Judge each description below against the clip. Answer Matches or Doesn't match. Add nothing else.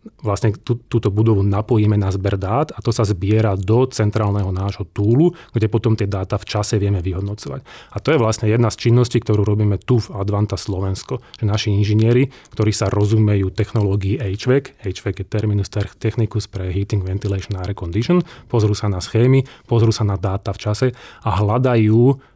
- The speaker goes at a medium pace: Doesn't match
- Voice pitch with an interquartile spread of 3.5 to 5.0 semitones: Doesn't match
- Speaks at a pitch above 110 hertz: Doesn't match